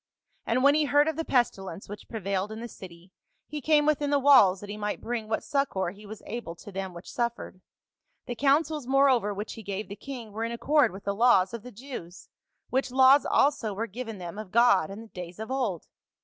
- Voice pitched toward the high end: Yes, high, 225 Hz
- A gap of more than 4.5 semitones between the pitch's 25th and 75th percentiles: Yes, average, 5.3 semitones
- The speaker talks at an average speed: No, fast, 220 wpm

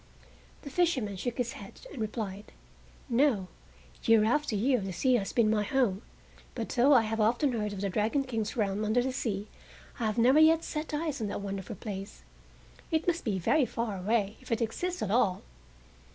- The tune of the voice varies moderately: Yes, average, 4.3 semitones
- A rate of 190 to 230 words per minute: Yes, average, 195 wpm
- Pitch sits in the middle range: No, high, 225 Hz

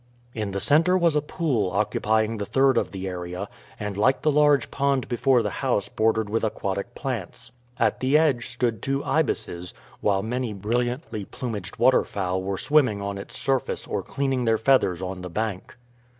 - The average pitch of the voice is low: Yes, low, 115 Hz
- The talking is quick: No, average, 175 wpm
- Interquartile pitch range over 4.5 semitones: Yes, average, 5.2 semitones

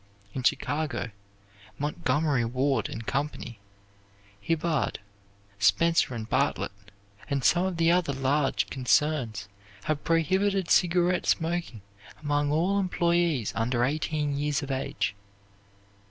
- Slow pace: Yes, slow, 110 wpm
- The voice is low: No, medium, 150 Hz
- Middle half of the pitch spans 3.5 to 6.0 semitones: Yes, average, 4.2 semitones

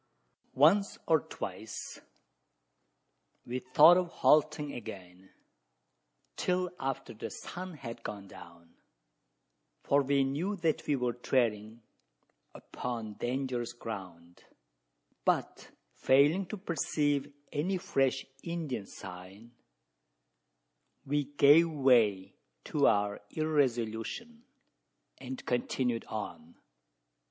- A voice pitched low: Yes, low, 130 Hz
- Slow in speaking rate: Yes, slow, 90 wpm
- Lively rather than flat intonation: Yes, wide, 6.0 semitones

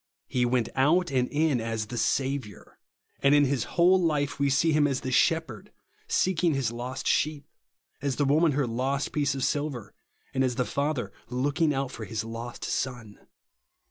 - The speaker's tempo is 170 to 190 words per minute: Yes, average, 175 wpm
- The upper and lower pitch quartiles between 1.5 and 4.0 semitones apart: Yes, average, 3.1 semitones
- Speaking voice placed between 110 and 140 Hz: Yes, low, 135 Hz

